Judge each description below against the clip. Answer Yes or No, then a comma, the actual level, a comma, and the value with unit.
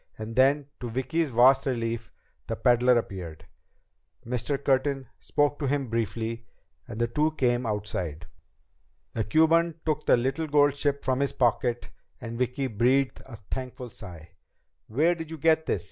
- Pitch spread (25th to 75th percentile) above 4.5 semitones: No, average, 3.9 semitones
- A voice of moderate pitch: No, low, 125 Hz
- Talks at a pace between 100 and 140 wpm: No, average, 155 wpm